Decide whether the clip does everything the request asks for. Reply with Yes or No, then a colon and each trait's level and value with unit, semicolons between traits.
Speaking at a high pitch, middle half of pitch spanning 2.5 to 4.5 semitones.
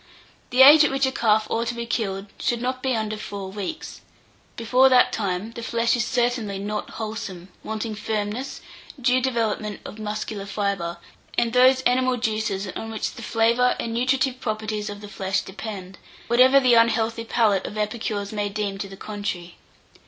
Yes: high, 220 Hz; average, 3.0 semitones